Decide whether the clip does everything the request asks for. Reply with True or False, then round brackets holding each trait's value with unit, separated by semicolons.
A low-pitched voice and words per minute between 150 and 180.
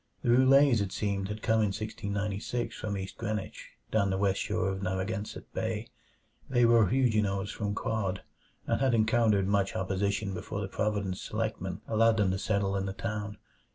True (105 Hz; 170 wpm)